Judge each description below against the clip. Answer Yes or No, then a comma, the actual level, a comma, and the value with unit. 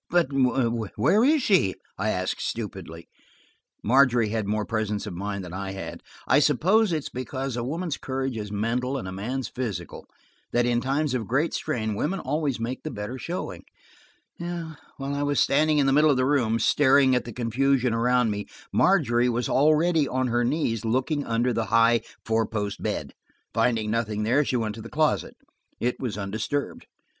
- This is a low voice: Yes, low, 125 Hz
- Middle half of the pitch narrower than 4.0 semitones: No, average, 4.3 semitones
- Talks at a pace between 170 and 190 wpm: Yes, average, 175 wpm